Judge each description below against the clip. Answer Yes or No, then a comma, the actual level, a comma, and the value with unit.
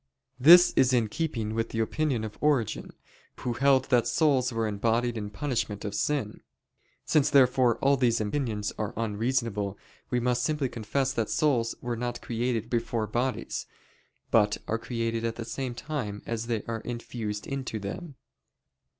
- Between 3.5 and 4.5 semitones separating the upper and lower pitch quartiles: No, average, 3.0 semitones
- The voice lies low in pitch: Yes, low, 120 Hz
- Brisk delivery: No, average, 160 wpm